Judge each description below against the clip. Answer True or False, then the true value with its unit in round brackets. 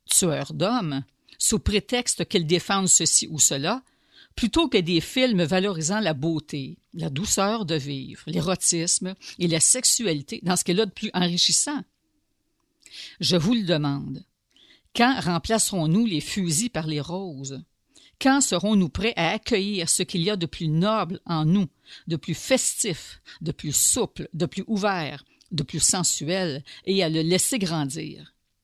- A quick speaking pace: False (155 wpm)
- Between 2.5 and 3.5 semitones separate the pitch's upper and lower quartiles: False (4.7 semitones)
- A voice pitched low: False (180 Hz)